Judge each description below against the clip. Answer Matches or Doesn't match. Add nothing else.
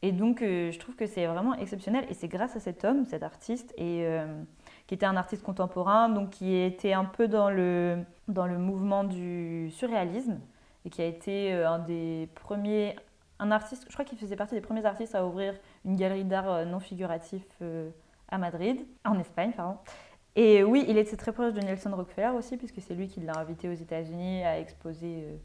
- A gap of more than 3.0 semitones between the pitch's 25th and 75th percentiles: Matches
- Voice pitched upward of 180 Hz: Matches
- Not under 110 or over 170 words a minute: Doesn't match